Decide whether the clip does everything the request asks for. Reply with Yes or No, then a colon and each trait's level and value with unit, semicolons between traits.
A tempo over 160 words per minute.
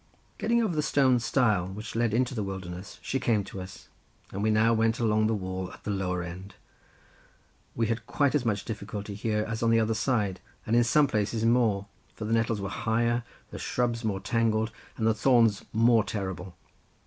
Yes: average, 195 wpm